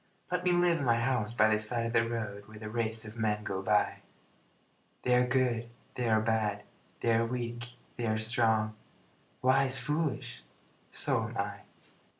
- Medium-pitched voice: No, low, 115 Hz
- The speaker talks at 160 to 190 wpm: Yes, average, 175 wpm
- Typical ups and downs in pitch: No, narrow, 2.3 semitones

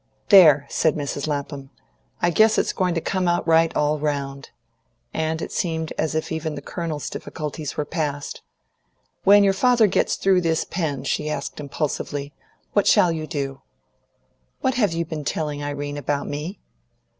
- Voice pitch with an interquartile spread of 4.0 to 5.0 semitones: No, average, 3.0 semitones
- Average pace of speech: Yes, average, 165 wpm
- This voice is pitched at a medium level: Yes, medium, 155 Hz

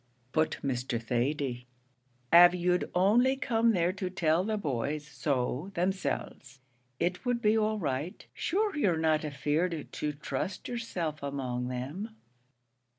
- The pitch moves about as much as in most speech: No, wide, 5.9 semitones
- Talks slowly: Yes, slow, 130 wpm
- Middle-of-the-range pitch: Yes, medium, 165 Hz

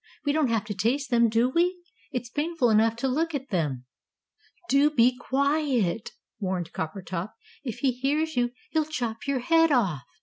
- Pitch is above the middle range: Yes, very high, 250 Hz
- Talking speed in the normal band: Yes, average, 170 wpm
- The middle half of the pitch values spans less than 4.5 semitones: No, average, 4.9 semitones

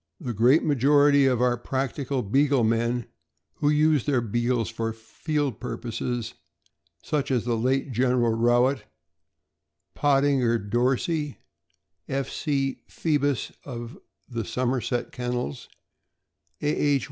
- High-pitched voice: No, low, 125 Hz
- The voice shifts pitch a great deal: No, average, 3.1 semitones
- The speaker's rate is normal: No, slow, 115 wpm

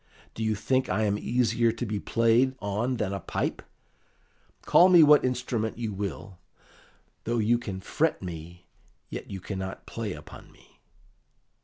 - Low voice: Yes, low, 110 Hz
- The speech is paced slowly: No, average, 155 wpm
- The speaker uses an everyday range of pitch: Yes, average, 3.7 semitones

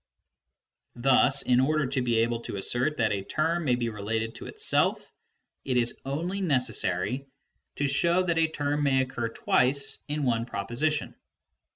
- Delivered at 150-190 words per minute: Yes, average, 160 wpm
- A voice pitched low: Yes, low, 130 Hz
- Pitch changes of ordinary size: Yes, average, 4.0 semitones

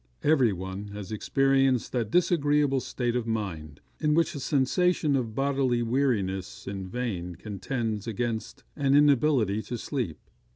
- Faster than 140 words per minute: No, slow, 135 wpm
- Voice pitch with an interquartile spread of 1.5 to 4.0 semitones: No, average, 5.0 semitones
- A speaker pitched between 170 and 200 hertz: No, low, 120 Hz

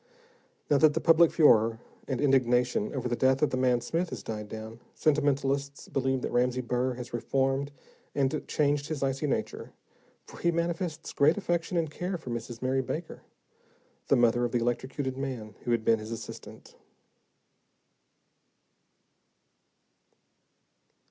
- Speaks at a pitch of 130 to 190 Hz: Yes, low, 135 Hz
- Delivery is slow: No, average, 145 wpm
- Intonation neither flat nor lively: Yes, average, 3.5 semitones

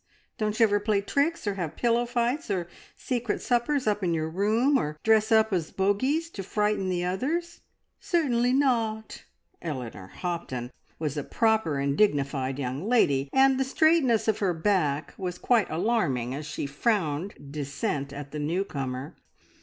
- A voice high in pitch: Yes, high, 200 Hz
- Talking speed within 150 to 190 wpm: Yes, average, 160 wpm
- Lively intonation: Yes, wide, 8.0 semitones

